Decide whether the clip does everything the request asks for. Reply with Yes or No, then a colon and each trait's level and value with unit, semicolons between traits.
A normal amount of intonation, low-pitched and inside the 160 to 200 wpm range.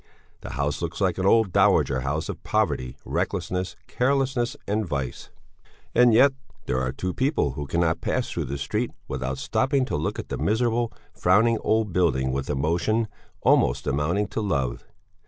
No: wide, 8.3 semitones; very low, 90 Hz; average, 165 wpm